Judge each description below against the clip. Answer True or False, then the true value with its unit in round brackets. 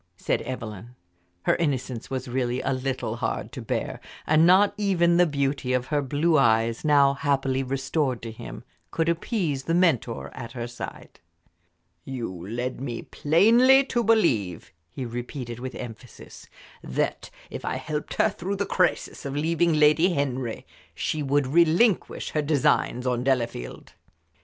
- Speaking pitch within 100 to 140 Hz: True (135 Hz)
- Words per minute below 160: True (150 wpm)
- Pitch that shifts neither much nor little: True (5.0 semitones)